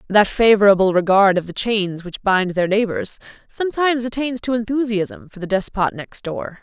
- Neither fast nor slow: Yes, average, 170 wpm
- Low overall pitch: No, high, 210 Hz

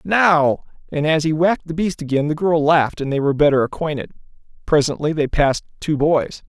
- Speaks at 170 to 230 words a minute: Yes, average, 190 wpm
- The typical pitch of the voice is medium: Yes, medium, 155 Hz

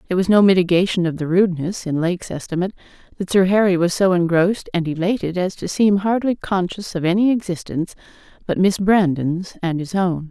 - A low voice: No, medium, 180 Hz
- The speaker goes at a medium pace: Yes, average, 185 wpm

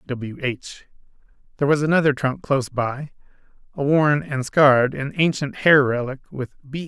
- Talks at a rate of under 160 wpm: Yes, average, 150 wpm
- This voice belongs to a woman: No, male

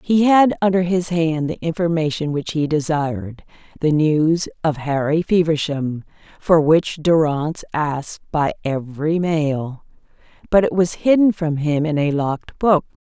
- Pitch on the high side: No, medium, 160 Hz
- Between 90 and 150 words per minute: Yes, average, 145 wpm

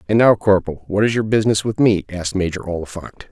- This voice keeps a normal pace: No, fast, 215 wpm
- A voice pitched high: No, low, 100 Hz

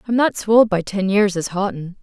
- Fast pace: Yes, fast, 265 wpm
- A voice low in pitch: No, high, 200 Hz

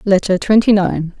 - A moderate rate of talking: Yes, average, 150 wpm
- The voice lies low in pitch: No, high, 195 Hz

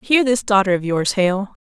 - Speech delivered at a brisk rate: Yes, fast, 215 wpm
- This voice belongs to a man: No, female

